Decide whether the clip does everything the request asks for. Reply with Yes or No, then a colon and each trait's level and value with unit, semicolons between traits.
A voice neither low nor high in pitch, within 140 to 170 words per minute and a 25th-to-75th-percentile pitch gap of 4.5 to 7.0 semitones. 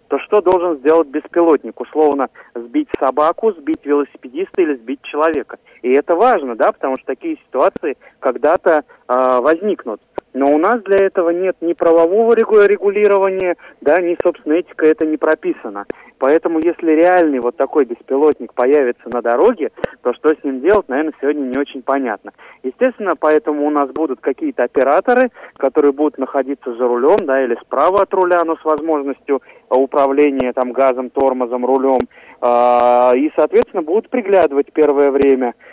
Yes: medium, 155 Hz; average, 155 wpm; wide, 5.5 semitones